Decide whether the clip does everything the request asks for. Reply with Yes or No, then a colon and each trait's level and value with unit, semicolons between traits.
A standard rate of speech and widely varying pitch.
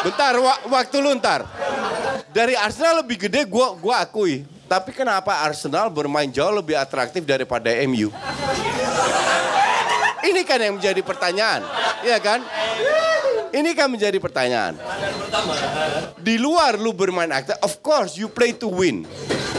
Yes: average, 130 wpm; wide, 7.0 semitones